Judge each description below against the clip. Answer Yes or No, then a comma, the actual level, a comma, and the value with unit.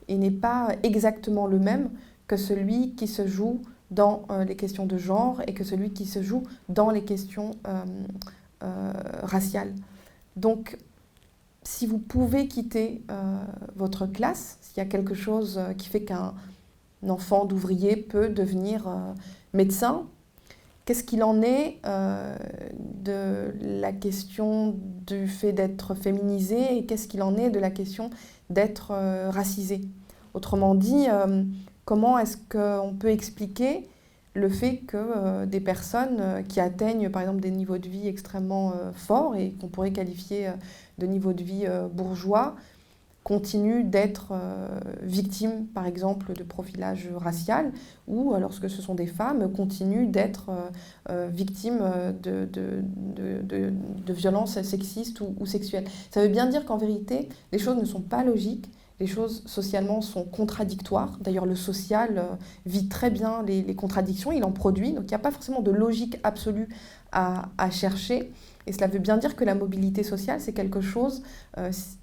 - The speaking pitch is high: Yes, high, 200 Hz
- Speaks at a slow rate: No, average, 160 wpm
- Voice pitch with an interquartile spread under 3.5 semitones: Yes, narrow, 2.4 semitones